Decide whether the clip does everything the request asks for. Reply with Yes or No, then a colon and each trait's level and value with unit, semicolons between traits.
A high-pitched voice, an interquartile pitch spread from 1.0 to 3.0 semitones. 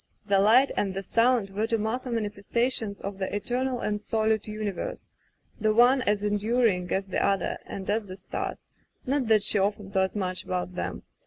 Yes: high, 210 Hz; average, 2.7 semitones